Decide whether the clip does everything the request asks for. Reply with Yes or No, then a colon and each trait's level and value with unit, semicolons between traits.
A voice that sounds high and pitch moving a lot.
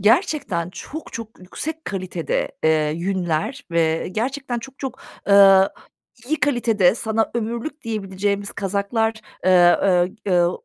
No: high, 205 Hz; average, 4.6 semitones